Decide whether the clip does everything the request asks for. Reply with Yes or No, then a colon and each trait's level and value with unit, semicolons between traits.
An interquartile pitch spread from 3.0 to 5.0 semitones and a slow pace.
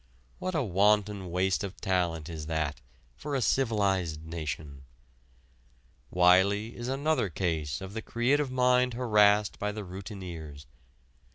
No: wide, 5.5 semitones; slow, 125 wpm